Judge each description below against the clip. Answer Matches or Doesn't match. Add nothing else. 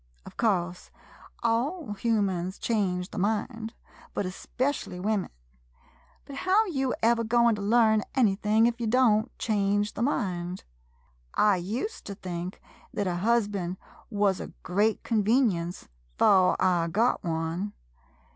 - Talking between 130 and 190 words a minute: Matches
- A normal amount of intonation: Matches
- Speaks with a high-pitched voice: Matches